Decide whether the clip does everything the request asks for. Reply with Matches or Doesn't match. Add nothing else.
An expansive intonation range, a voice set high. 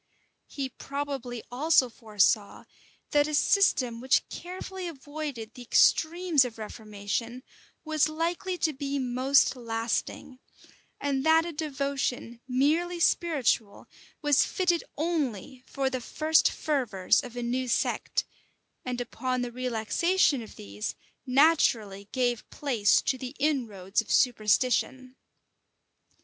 Doesn't match